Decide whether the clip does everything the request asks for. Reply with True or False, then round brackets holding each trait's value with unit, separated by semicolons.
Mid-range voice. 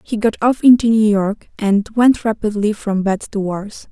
False (215 Hz)